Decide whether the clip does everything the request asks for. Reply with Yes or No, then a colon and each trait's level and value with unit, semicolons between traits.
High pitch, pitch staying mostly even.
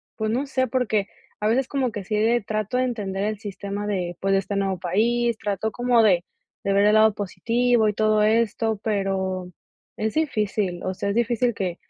No: high, 215 Hz; average, 3.0 semitones